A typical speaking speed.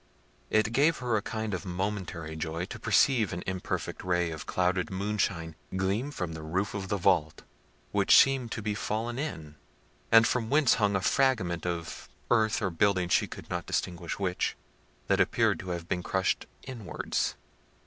Yes: average, 170 wpm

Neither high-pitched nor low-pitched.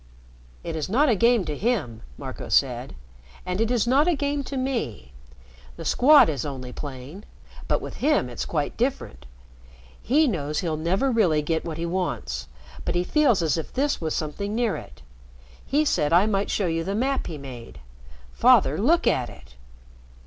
Yes: medium, 180 Hz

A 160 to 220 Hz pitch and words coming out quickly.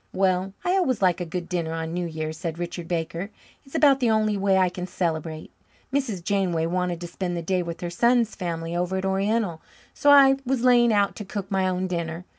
Yes: medium, 185 Hz; fast, 220 wpm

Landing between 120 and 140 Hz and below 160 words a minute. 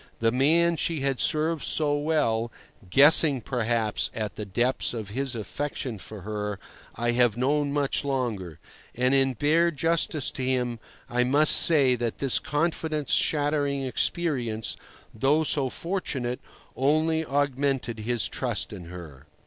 Yes: low, 135 Hz; average, 140 wpm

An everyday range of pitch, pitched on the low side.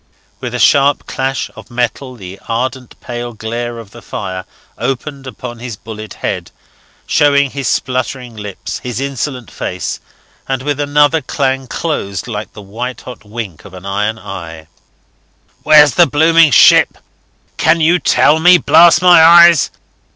Yes: average, 4.7 semitones; low, 125 Hz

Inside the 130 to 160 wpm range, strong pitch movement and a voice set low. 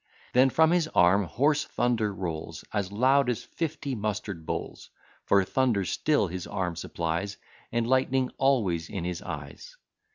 Yes: average, 150 wpm; wide, 6.4 semitones; low, 105 Hz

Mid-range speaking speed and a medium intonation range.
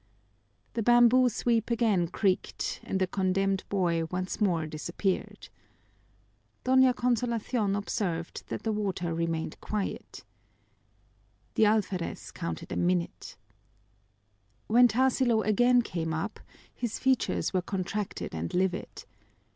No: slow, 110 wpm; average, 4.8 semitones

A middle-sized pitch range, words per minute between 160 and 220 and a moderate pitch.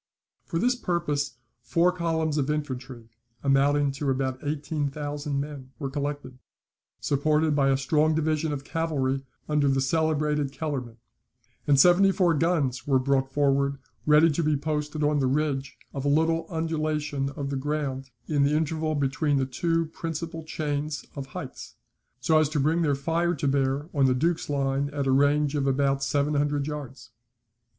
No: narrow, 2.3 semitones; average, 165 wpm; medium, 145 Hz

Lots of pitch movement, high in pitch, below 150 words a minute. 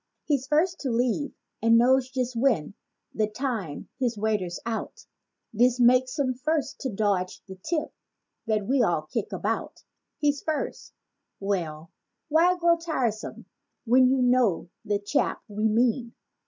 No: average, 4.2 semitones; high, 245 Hz; average, 140 wpm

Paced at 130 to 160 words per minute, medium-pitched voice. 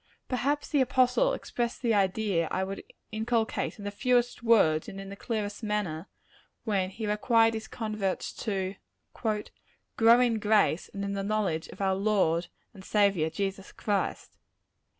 No: average, 150 wpm; high, 210 Hz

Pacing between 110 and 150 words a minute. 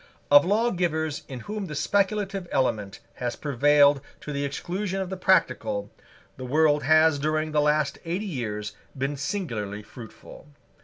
Yes: average, 145 wpm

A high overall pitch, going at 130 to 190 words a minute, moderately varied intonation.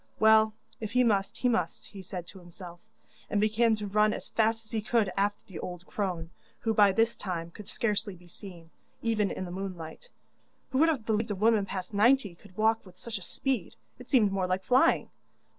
No: high, 205 Hz; fast, 205 wpm; average, 3.3 semitones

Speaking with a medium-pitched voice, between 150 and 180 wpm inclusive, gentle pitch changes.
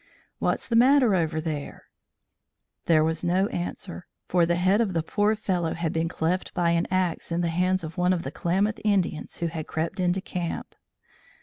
No: medium, 175 Hz; average, 190 wpm; narrow, 2.2 semitones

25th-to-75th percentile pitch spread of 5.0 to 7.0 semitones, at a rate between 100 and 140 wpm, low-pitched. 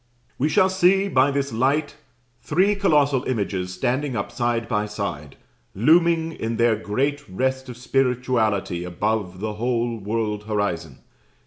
Yes: average, 5.3 semitones; slow, 135 wpm; low, 120 Hz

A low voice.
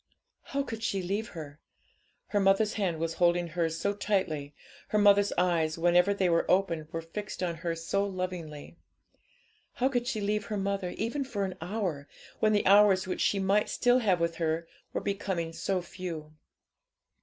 No: medium, 185 Hz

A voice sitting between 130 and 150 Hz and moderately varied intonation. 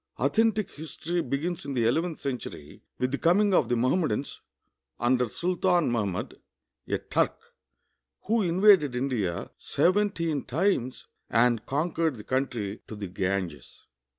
No: medium, 140 Hz; wide, 6.9 semitones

